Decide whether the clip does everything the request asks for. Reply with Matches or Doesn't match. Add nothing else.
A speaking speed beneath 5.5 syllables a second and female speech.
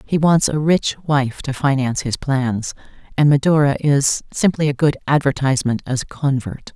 Matches